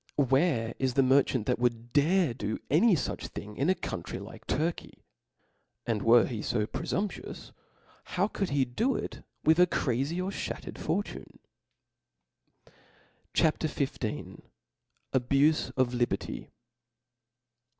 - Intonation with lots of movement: Yes, wide, 5.7 semitones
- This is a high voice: No, low, 135 Hz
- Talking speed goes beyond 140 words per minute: No, slow, 135 wpm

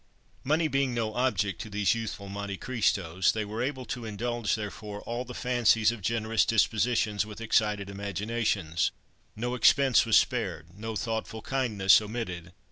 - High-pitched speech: No, low, 110 Hz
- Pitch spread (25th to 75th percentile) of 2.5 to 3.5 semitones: Yes, average, 2.8 semitones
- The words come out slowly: No, average, 150 wpm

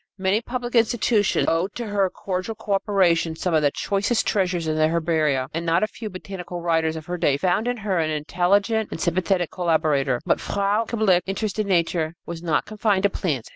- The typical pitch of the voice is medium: Yes, medium, 180 Hz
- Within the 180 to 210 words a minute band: Yes, average, 195 wpm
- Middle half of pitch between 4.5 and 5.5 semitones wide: No, average, 3.9 semitones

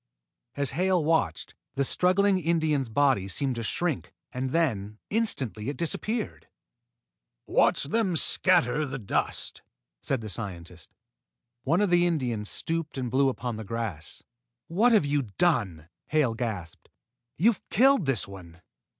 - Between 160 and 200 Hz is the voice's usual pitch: No, low, 135 Hz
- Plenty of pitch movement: Yes, wide, 7.6 semitones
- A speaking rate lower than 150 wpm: Yes, slow, 135 wpm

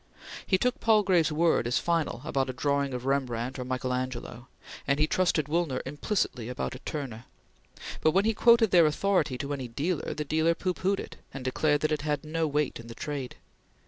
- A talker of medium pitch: Yes, medium, 145 Hz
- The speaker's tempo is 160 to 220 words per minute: Yes, average, 200 wpm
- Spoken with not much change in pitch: No, average, 4.7 semitones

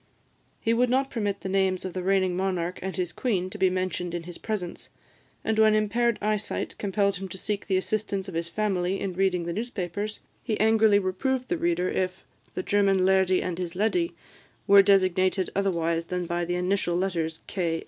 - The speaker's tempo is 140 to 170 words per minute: No, average, 190 wpm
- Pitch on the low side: No, high, 190 Hz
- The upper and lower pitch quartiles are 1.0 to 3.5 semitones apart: Yes, average, 2.7 semitones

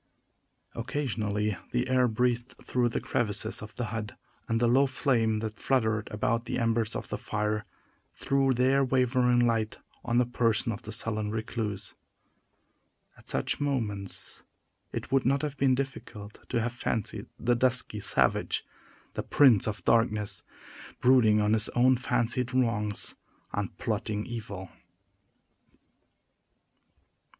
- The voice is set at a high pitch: No, low, 115 Hz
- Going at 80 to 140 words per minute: Yes, slow, 135 wpm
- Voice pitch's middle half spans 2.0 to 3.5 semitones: Yes, average, 2.9 semitones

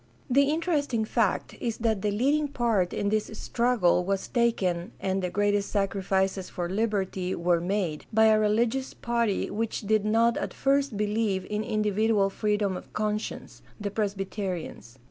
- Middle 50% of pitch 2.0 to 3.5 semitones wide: Yes, average, 2.9 semitones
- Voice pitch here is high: Yes, high, 210 Hz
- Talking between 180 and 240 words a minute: No, average, 155 wpm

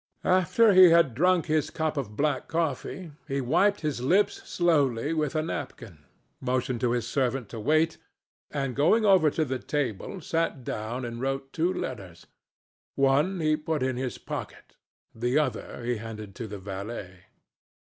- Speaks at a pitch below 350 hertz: Yes, low, 135 Hz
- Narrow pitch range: No, average, 5.2 semitones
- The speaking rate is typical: Yes, average, 160 wpm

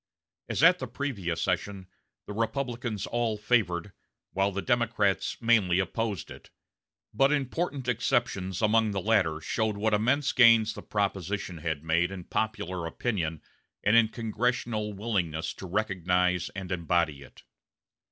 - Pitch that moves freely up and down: No, average, 4.2 semitones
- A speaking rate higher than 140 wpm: No, slow, 135 wpm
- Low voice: Yes, low, 105 Hz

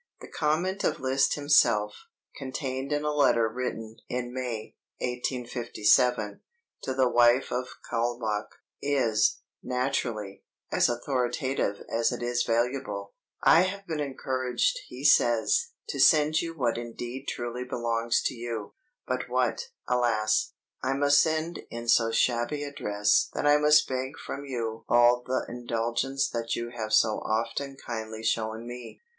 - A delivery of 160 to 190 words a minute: No, average, 140 wpm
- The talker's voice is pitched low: Yes, low, 125 Hz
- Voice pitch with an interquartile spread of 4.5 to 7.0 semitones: No, average, 3.0 semitones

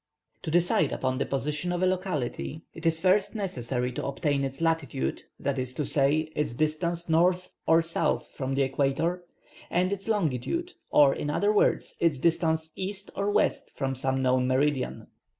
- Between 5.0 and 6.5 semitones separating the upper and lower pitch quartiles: No, average, 4.5 semitones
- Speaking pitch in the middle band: Yes, medium, 155 Hz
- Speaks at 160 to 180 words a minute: Yes, average, 170 wpm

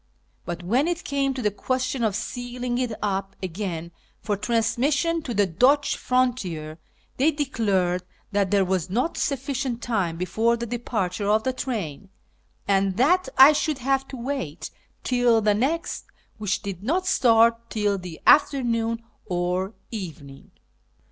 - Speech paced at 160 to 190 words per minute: No, average, 145 wpm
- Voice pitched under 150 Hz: No, high, 230 Hz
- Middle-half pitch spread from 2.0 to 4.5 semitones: No, average, 5.1 semitones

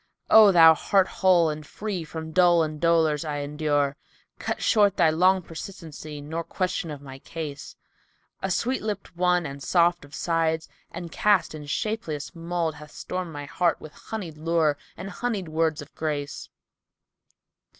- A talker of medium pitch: Yes, medium, 165 Hz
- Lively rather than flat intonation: No, average, 3.1 semitones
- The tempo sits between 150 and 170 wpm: Yes, average, 165 wpm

